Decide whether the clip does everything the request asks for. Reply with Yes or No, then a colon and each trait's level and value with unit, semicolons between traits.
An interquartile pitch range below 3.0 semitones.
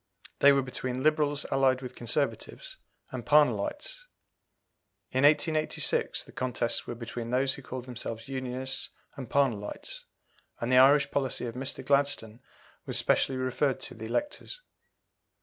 Yes: narrow, 2.5 semitones